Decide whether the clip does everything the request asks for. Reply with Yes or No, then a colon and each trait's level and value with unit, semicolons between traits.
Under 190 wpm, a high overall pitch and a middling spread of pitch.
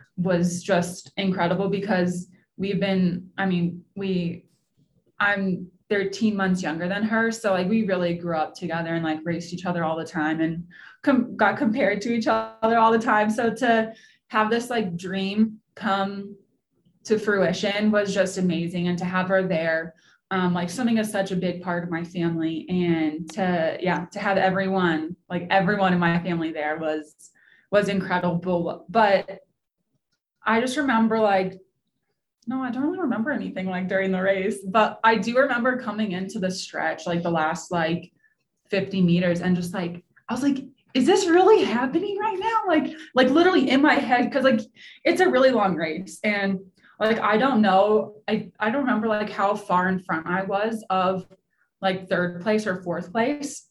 Yes: average, 180 wpm; high, 195 Hz; average, 3.9 semitones